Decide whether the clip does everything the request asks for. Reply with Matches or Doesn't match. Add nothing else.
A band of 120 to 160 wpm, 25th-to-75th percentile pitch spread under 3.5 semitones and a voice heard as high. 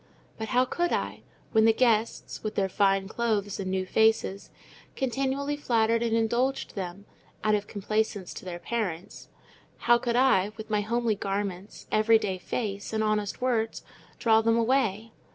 Matches